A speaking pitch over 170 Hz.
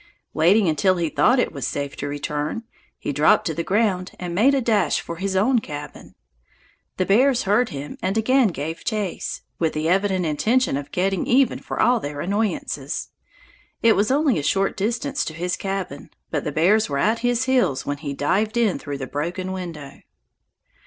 Yes: medium, 185 Hz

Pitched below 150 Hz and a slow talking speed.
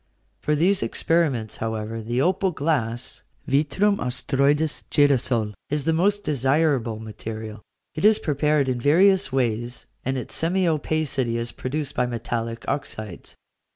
Yes: low, 135 Hz; slow, 130 wpm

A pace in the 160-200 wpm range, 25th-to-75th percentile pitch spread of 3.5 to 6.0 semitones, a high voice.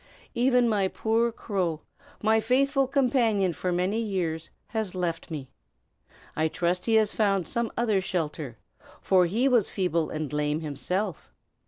No: average, 145 wpm; average, 5.3 semitones; high, 195 Hz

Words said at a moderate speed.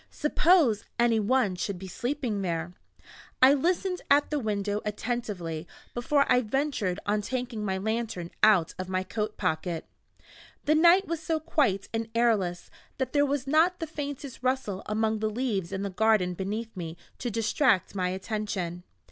Yes: average, 155 wpm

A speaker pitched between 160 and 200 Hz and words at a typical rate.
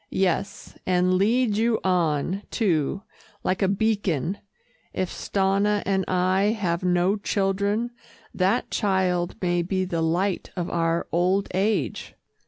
No: high, 190 Hz; slow, 125 wpm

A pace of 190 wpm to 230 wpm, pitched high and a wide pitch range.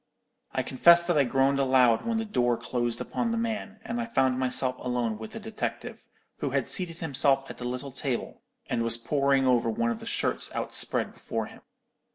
No: average, 200 wpm; low, 135 Hz; wide, 5.8 semitones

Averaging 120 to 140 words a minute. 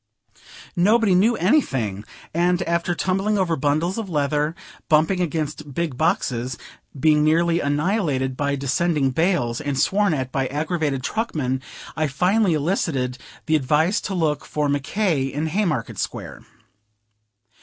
Yes: slow, 135 wpm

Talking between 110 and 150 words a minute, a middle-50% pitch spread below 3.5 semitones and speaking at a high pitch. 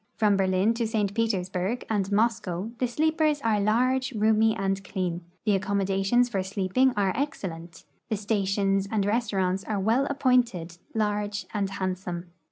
Yes: average, 145 wpm; average, 3.1 semitones; high, 205 Hz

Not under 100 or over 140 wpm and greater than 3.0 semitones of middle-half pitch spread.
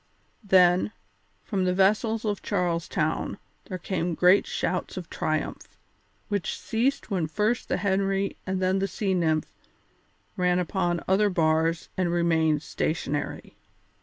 No: slow, 135 wpm; average, 2.7 semitones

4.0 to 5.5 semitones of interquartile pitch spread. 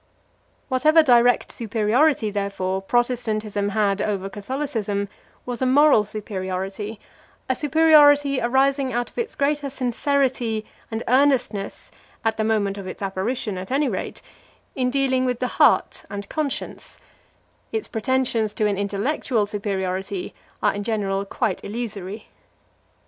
Yes: average, 4.5 semitones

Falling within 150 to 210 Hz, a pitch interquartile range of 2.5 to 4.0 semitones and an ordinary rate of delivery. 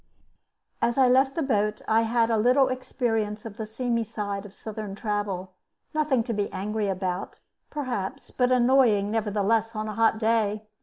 No: high, 220 Hz; average, 3.0 semitones; average, 165 wpm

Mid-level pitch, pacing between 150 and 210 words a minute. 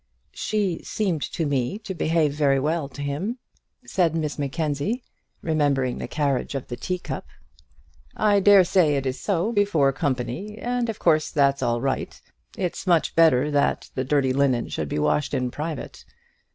Yes: medium, 150 Hz; average, 165 wpm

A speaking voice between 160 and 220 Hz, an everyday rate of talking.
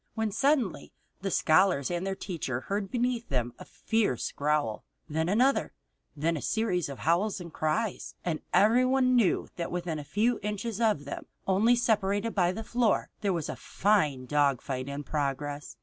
Yes: medium, 185 Hz; average, 165 wpm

